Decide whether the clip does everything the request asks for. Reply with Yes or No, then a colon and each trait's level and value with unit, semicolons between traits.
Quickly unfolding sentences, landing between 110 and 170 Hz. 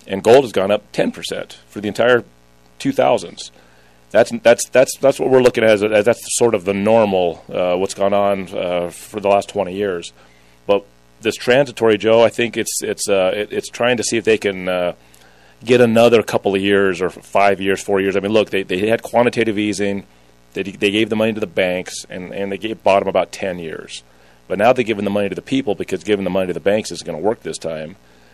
No: fast, 235 wpm; low, 100 Hz